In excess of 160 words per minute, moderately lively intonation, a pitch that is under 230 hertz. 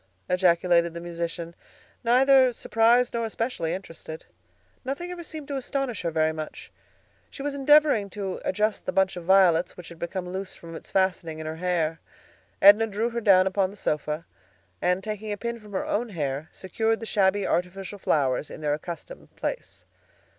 Yes: average, 175 wpm; average, 5.0 semitones; high, 190 Hz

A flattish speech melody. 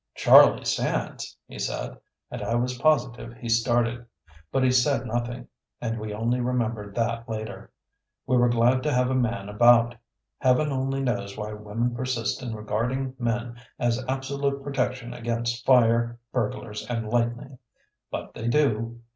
Yes: narrow, 1.8 semitones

